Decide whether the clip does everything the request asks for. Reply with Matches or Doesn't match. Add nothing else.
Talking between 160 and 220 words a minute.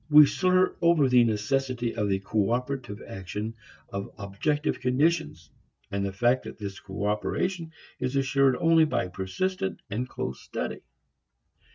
Doesn't match